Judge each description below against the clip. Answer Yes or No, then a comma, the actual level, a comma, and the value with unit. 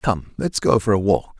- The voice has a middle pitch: No, low, 100 Hz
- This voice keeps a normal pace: No, fast, 260 wpm